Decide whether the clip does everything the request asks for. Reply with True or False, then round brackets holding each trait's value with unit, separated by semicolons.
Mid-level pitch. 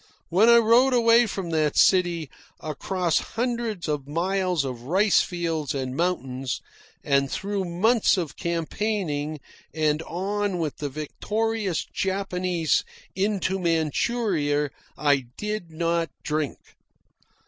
True (175 Hz)